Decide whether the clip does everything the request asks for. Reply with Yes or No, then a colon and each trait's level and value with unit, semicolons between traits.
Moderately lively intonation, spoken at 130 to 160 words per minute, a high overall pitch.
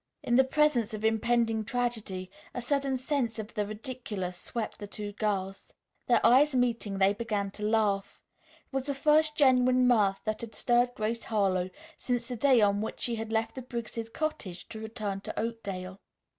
No: average, 3.1 semitones; average, 180 wpm; high, 225 Hz